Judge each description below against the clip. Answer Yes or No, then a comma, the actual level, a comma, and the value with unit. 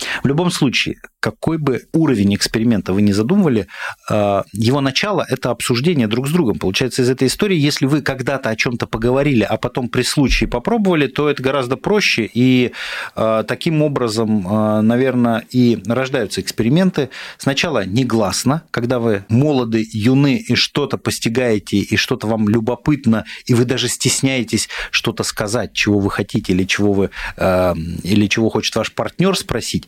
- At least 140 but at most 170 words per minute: Yes, fast, 160 wpm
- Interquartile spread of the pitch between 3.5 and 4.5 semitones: Yes, average, 3.8 semitones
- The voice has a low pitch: Yes, low, 120 Hz